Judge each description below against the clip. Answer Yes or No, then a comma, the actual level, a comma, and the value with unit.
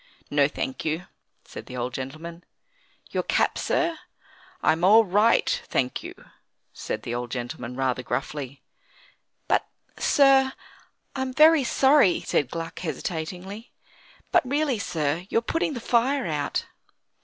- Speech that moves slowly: Yes, slow, 130 wpm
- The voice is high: No, medium, 180 Hz